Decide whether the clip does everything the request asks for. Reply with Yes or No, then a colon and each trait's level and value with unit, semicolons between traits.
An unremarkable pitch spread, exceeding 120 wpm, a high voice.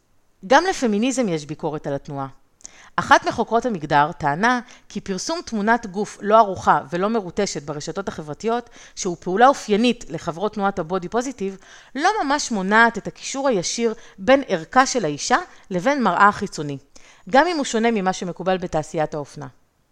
No: wide, 6.4 semitones; average, 145 wpm; high, 200 Hz